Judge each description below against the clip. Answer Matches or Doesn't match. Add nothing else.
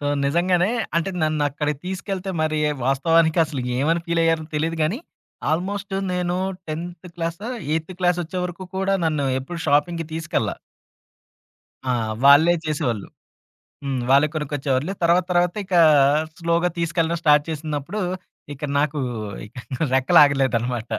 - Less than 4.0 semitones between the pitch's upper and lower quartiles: Matches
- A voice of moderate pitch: Matches